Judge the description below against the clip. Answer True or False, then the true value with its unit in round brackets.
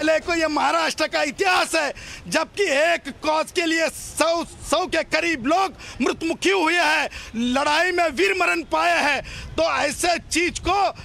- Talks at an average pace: False (160 wpm)